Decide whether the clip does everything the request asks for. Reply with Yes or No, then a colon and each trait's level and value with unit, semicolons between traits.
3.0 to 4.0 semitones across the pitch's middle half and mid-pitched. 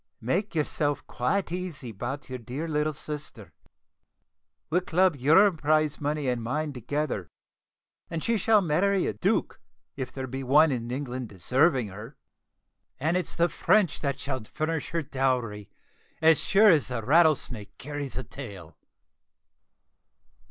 No: average, 4.4 semitones; medium, 145 Hz